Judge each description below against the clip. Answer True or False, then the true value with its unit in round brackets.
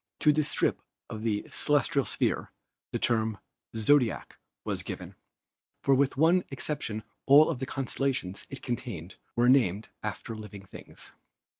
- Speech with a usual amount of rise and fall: True (4.4 semitones)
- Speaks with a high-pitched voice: False (125 Hz)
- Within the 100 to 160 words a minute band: True (140 wpm)